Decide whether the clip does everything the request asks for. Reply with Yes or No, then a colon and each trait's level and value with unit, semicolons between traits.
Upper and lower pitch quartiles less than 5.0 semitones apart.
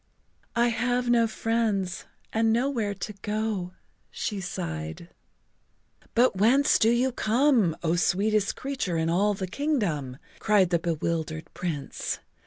No: average, 5.3 semitones